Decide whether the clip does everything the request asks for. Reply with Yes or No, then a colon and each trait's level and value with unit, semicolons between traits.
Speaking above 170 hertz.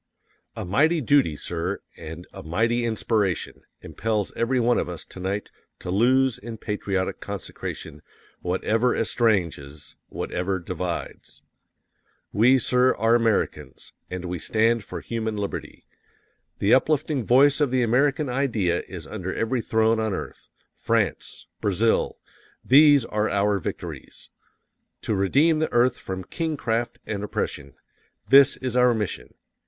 No: low, 110 Hz